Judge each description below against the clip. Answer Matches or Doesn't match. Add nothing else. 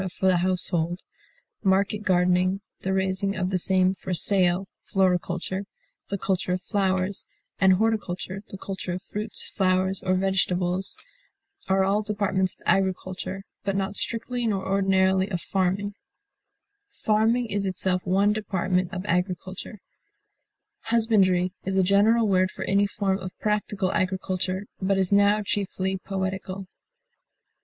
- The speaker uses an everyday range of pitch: Doesn't match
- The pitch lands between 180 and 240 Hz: Matches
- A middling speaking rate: Doesn't match